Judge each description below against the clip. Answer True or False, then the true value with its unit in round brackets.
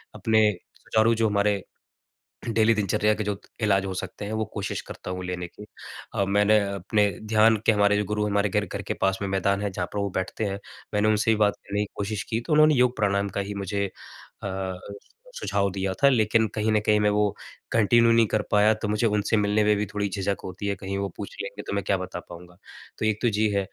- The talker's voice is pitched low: True (105 Hz)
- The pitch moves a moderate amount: False (1.6 semitones)